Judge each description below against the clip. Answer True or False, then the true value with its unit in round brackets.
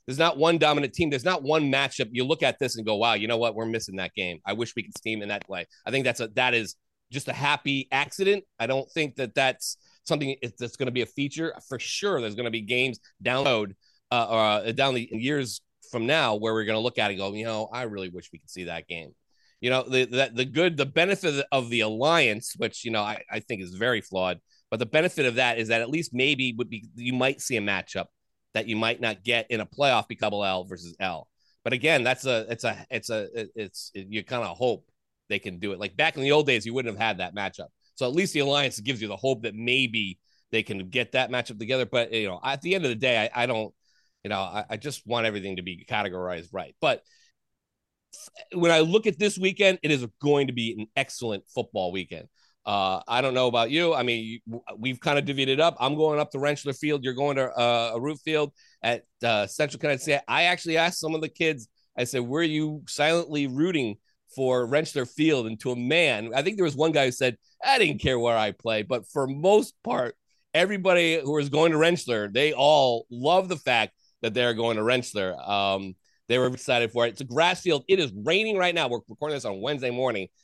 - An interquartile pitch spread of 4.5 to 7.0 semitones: True (5.0 semitones)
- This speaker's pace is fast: True (245 wpm)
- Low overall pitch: True (125 Hz)